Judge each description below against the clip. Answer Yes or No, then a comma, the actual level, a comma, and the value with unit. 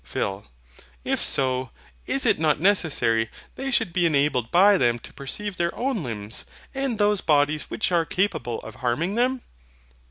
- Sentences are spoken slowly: No, average, 160 wpm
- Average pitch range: No, wide, 8.5 semitones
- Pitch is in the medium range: Yes, medium, 160 Hz